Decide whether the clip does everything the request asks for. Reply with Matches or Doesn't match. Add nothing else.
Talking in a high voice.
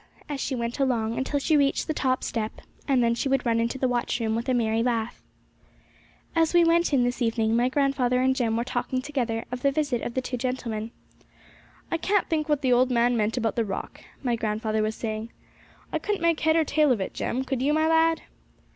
Matches